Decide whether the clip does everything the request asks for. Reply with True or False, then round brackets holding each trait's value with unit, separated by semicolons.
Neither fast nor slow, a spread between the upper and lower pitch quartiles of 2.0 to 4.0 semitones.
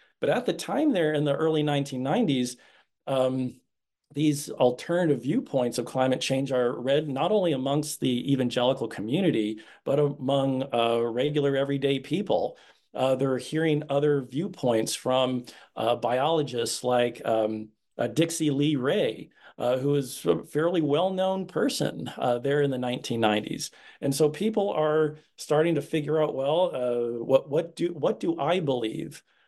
True (150 wpm; 3.5 semitones)